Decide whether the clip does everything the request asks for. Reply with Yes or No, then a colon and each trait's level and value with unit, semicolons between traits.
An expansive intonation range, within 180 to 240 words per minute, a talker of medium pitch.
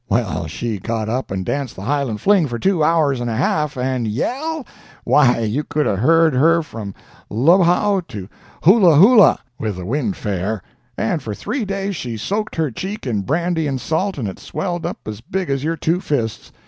Yes: wide, 7.6 semitones; average, 190 wpm; medium, 145 Hz